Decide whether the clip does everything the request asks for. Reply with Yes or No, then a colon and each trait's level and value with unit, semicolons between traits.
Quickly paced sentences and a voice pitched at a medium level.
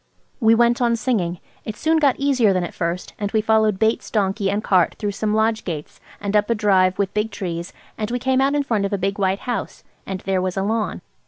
No: fast, 240 wpm; high, 210 Hz